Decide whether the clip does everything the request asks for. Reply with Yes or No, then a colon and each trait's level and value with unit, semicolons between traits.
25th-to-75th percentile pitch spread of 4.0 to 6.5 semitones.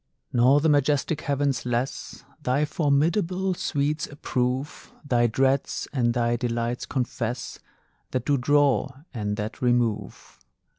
No: average, 3.3 semitones